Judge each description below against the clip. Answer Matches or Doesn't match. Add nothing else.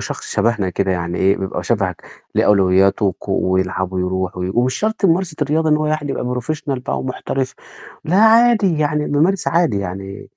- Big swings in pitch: Matches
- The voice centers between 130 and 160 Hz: Doesn't match